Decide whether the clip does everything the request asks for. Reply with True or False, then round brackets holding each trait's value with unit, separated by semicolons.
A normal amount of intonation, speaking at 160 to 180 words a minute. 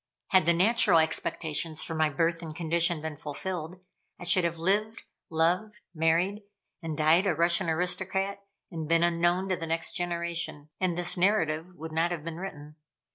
False (2.2 semitones; 170 wpm)